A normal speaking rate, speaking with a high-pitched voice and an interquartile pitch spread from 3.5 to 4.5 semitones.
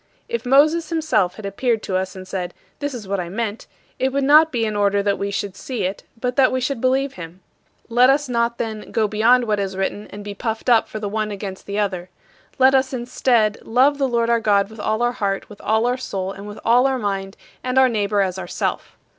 No: fast, 240 wpm; high, 220 Hz; average, 4.1 semitones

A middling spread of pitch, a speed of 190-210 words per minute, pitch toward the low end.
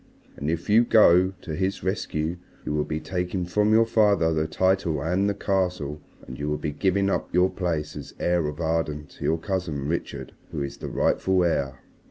Yes: average, 3.8 semitones; average, 200 wpm; very low, 85 Hz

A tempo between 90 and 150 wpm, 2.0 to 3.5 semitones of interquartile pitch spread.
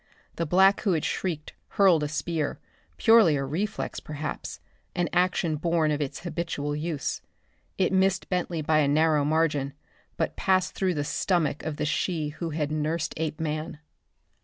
No: average, 160 wpm; average, 2.9 semitones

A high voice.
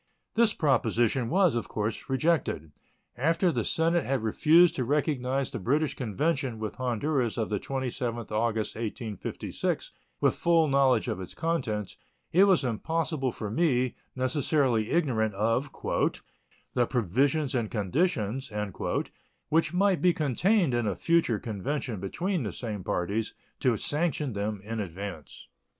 No: low, 130 Hz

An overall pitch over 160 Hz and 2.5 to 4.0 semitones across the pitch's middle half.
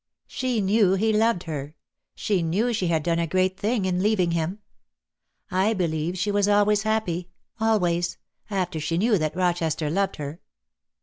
Yes: medium, 185 Hz; average, 3.7 semitones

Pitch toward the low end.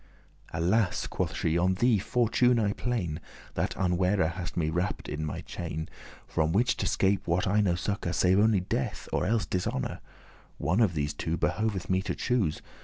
Yes: very low, 95 Hz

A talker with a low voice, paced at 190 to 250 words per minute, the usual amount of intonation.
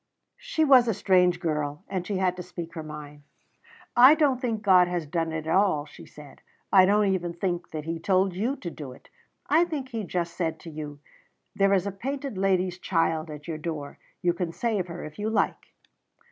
No: medium, 180 Hz; fast, 205 wpm; average, 4.2 semitones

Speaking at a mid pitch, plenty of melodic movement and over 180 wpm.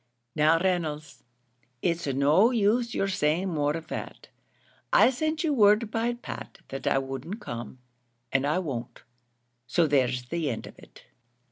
No: medium, 165 Hz; wide, 7.0 semitones; average, 150 wpm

